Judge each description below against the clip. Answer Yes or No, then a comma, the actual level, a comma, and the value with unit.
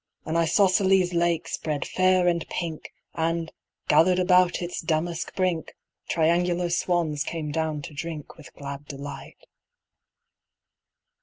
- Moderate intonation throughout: No, narrow, 2.2 semitones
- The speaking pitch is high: No, medium, 170 Hz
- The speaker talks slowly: Yes, slow, 120 wpm